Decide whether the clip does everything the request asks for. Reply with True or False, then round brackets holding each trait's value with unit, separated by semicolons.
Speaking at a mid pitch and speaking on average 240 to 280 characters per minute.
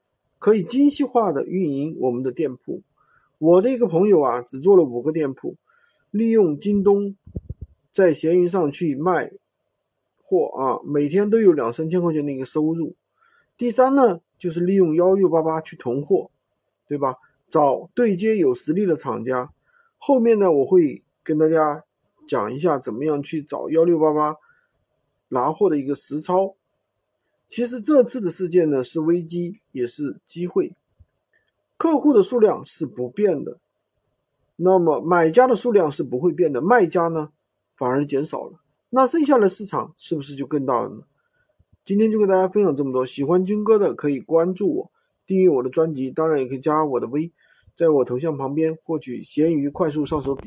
True (170 Hz; 255 characters per minute)